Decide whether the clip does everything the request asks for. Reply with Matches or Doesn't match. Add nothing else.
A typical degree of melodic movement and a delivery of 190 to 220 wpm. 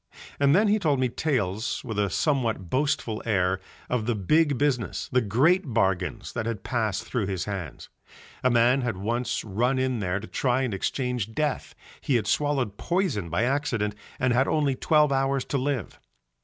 Doesn't match